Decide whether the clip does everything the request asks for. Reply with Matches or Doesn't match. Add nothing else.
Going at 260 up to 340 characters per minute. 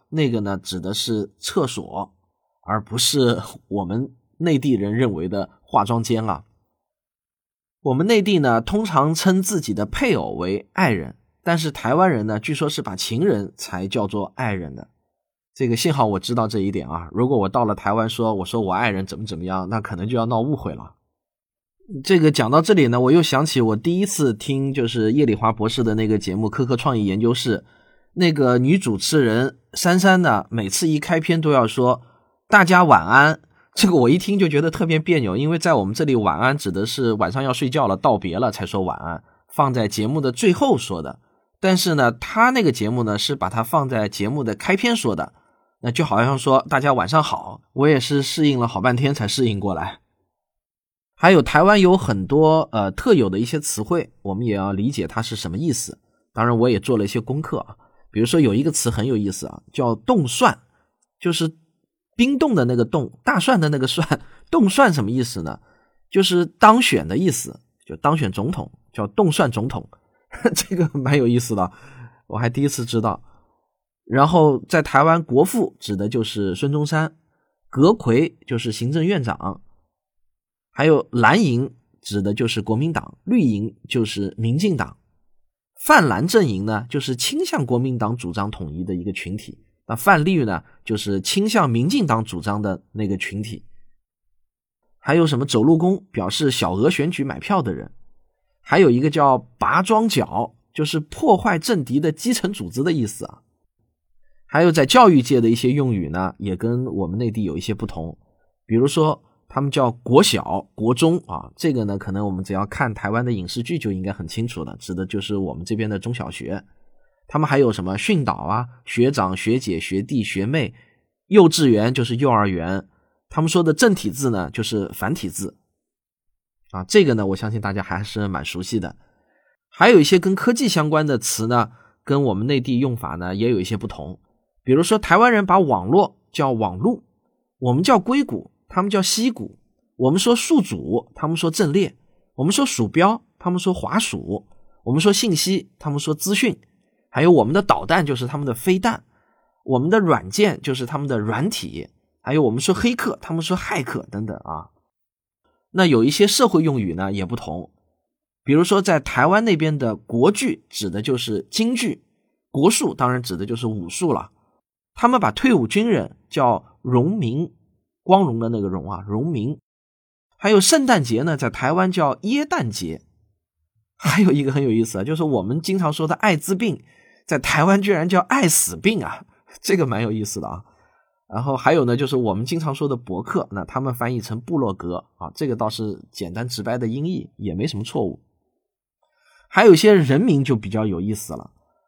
Matches